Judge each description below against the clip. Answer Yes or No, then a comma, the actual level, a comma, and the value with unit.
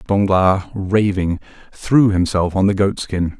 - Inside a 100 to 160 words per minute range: Yes, average, 140 wpm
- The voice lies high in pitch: No, very low, 95 Hz